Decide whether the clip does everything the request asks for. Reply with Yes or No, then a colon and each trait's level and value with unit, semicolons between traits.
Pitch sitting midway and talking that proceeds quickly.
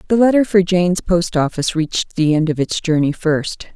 Yes: medium, 175 Hz; fast, 210 wpm